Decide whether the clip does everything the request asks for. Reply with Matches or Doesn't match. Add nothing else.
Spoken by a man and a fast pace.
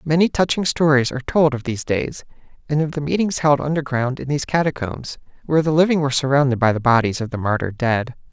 Matches